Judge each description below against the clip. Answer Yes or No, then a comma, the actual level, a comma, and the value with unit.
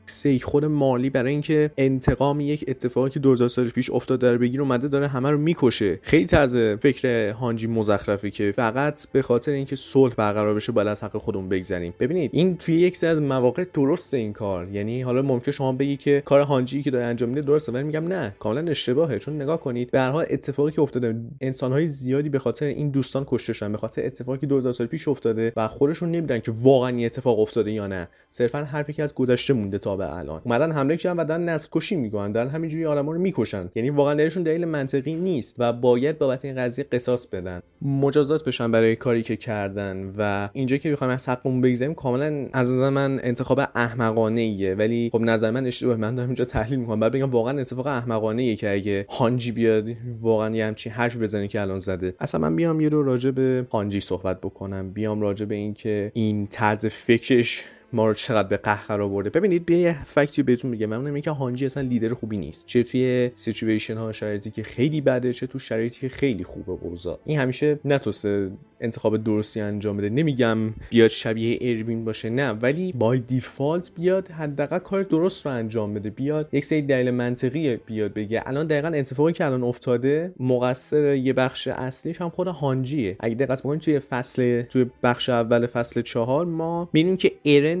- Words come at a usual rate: No, fast, 200 wpm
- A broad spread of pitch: No, average, 4.2 semitones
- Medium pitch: No, low, 125 Hz